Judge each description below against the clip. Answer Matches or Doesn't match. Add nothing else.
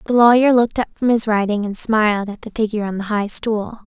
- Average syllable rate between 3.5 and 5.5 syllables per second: Doesn't match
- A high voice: Matches